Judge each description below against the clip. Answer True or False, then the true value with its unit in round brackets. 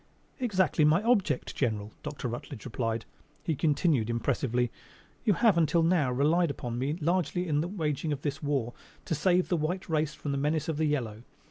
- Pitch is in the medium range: True (150 Hz)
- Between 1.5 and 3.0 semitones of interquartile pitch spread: False (4.9 semitones)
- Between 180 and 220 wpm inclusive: True (185 wpm)